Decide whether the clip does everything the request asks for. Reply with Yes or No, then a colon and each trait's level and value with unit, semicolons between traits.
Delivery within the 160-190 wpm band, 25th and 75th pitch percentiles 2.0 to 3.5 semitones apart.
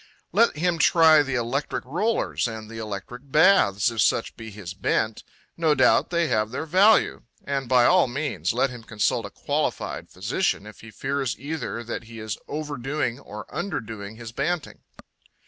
No: average, 165 wpm; wide, 5.6 semitones